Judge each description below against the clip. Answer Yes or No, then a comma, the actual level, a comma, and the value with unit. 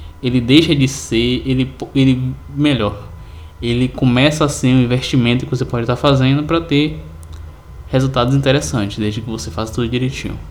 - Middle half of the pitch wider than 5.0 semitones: No, average, 3.7 semitones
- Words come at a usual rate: Yes, average, 160 wpm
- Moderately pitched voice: No, low, 125 Hz